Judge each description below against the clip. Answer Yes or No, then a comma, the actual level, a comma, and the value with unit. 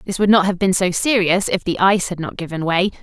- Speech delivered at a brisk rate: Yes, fast, 280 wpm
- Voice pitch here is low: No, medium, 185 Hz